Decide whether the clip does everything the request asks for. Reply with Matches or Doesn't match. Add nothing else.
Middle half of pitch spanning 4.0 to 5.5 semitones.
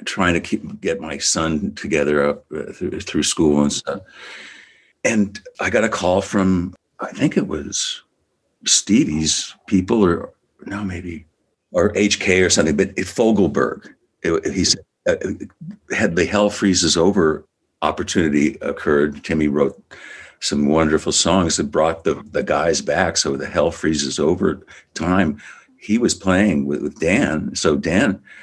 Matches